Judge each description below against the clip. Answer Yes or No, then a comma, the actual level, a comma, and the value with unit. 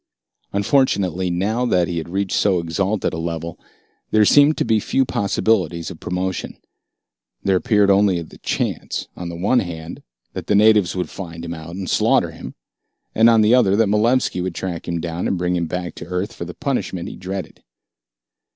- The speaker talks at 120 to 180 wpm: No, average, 190 wpm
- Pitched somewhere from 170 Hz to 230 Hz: No, very low, 95 Hz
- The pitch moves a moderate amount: Yes, average, 3.6 semitones